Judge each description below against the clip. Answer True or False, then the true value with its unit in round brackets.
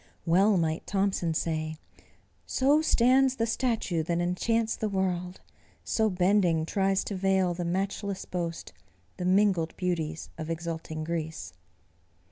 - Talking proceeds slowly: True (125 wpm)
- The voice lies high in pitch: False (180 Hz)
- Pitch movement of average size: True (3.4 semitones)